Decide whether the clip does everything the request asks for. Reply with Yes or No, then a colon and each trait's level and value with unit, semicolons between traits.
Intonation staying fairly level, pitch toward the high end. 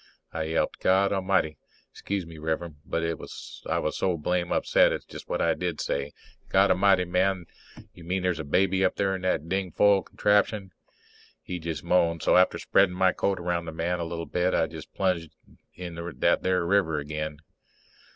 No: narrow, 2.3 semitones; very low, 90 Hz